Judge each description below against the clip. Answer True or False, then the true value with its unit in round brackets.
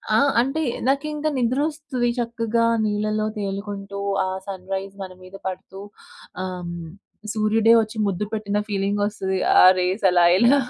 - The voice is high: True (210 Hz)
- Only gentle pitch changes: False (3.1 semitones)